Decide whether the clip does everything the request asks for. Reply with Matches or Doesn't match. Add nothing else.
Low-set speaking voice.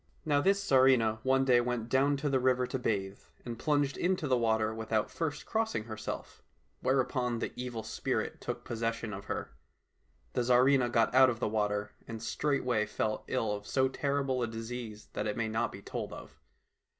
Matches